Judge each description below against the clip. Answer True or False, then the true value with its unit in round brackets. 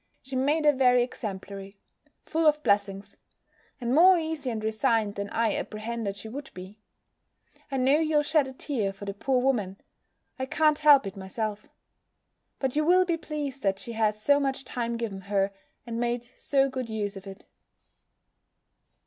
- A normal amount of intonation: False (5.7 semitones)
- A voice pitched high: True (240 Hz)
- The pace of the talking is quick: False (170 wpm)